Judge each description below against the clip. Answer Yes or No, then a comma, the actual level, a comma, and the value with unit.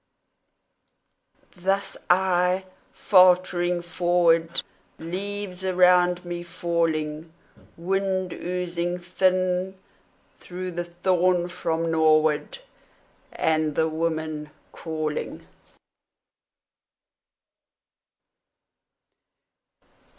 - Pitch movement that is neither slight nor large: No, narrow, 1.9 semitones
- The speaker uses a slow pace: Yes, slow, 60 wpm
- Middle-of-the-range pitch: Yes, medium, 175 Hz